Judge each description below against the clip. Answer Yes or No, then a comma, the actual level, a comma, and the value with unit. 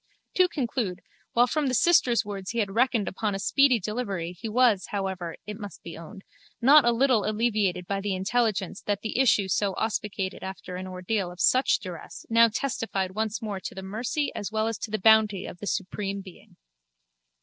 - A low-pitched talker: No, high, 210 Hz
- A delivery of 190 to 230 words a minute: Yes, average, 195 wpm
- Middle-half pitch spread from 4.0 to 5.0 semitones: No, average, 3.5 semitones